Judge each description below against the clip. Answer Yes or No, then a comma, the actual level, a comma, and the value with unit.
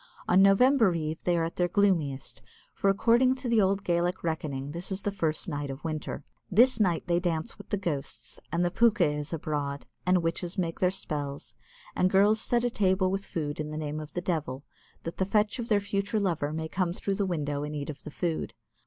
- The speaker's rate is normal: No, fast, 220 wpm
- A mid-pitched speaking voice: Yes, medium, 175 Hz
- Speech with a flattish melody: No, average, 4.4 semitones